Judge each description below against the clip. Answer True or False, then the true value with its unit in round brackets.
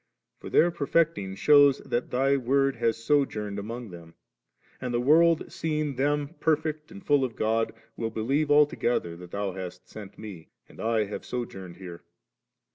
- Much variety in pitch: True (6.1 semitones)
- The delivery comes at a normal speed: True (160 wpm)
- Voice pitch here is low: True (125 Hz)